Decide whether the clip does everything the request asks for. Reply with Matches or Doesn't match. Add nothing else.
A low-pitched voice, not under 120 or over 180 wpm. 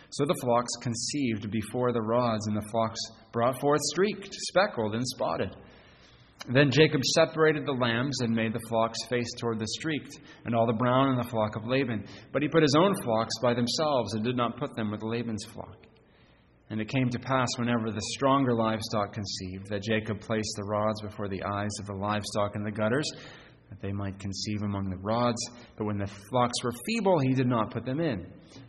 Doesn't match